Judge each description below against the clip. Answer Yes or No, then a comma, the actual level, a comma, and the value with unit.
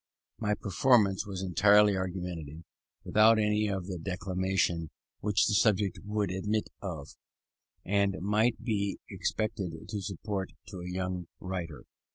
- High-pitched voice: No, very low, 95 Hz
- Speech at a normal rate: No, slow, 130 wpm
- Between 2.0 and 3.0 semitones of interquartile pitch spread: Yes, narrow, 2.5 semitones